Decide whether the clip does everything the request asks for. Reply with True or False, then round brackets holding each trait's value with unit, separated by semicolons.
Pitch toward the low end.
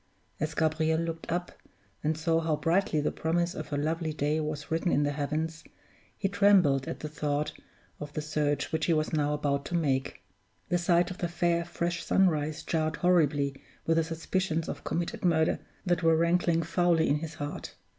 False (160 Hz)